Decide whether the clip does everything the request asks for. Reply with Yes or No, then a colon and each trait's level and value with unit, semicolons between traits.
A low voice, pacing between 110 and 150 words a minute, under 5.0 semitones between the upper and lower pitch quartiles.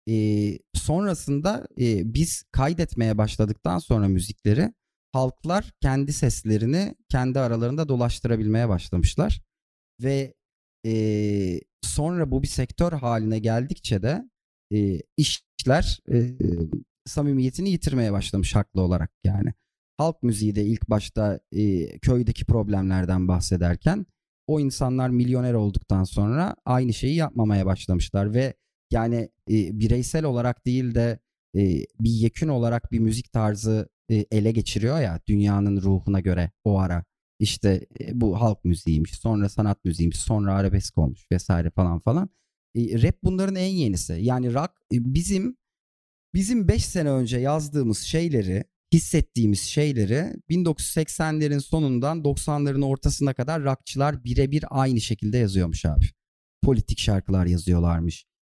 No: low, 115 Hz; average, 125 wpm; wide, 5.6 semitones